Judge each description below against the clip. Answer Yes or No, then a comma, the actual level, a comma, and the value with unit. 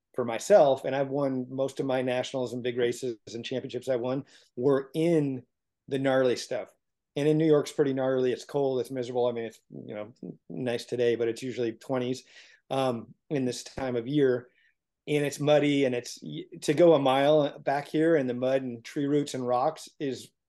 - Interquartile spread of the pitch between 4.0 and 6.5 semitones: No, narrow, 2.5 semitones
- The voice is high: No, low, 130 Hz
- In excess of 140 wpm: Yes, average, 200 wpm